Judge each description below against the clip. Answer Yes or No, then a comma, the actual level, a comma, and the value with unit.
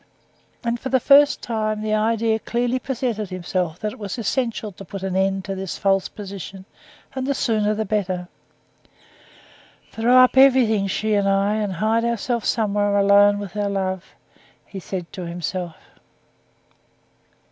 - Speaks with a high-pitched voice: Yes, high, 205 Hz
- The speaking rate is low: No, average, 155 wpm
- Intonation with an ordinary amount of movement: Yes, average, 3.0 semitones